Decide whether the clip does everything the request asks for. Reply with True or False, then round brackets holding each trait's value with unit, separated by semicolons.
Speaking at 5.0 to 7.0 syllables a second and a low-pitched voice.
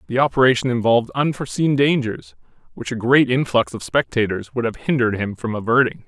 True (6.0 syllables/s; 120 Hz)